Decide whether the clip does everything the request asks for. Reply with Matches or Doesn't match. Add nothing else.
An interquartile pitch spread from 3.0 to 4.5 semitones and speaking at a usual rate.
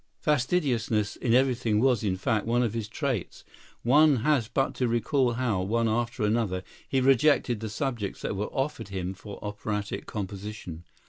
Matches